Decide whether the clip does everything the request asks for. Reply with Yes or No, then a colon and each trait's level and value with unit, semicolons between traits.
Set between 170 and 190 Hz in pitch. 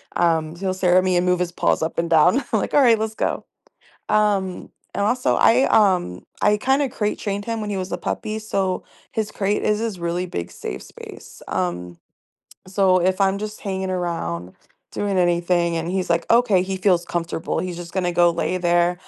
Yes: medium, 185 Hz